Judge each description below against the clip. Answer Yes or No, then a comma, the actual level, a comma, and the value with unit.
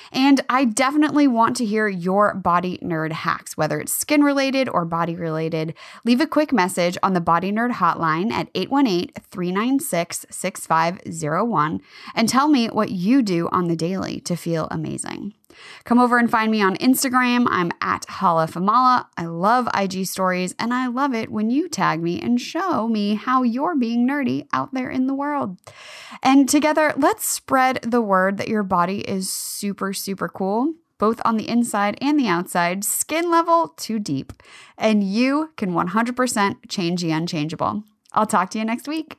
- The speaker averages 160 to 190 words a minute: Yes, average, 175 wpm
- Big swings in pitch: Yes, wide, 6.3 semitones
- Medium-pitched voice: No, high, 220 Hz